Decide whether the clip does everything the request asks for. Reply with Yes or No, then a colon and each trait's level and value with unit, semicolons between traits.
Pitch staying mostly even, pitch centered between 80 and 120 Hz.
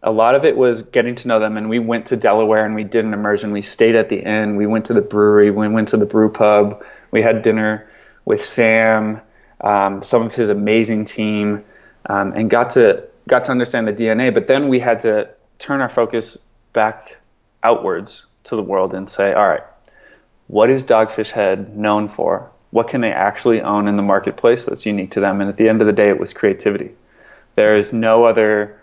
Yes: narrow, 1.4 semitones; low, 110 Hz